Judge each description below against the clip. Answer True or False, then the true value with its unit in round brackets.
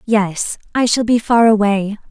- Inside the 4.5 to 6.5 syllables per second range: False (4.1 syllables/s)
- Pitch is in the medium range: False (215 Hz)